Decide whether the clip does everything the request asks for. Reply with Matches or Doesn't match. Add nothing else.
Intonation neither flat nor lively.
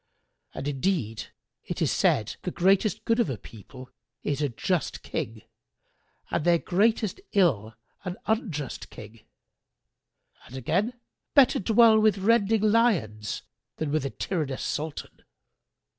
Doesn't match